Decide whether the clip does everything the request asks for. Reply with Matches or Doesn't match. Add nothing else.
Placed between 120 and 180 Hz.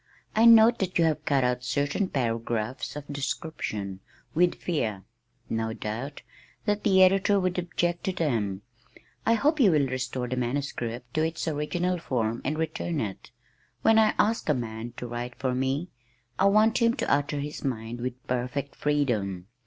Matches